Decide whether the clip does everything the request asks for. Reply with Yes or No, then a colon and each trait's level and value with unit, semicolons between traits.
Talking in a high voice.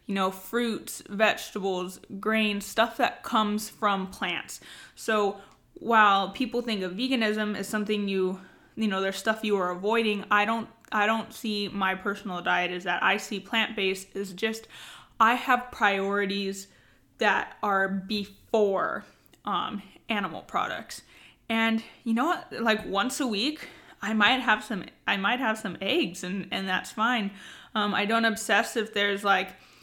Yes: high, 210 Hz